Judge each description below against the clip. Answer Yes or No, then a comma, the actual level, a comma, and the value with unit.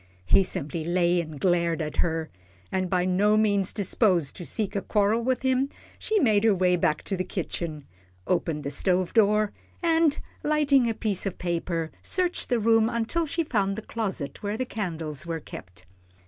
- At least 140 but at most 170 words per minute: No, average, 180 wpm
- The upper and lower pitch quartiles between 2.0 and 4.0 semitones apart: No, average, 4.9 semitones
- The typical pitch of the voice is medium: No, high, 195 Hz